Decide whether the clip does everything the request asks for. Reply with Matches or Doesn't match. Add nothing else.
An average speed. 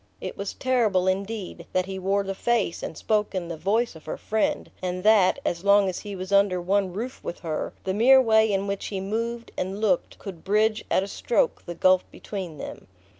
Doesn't match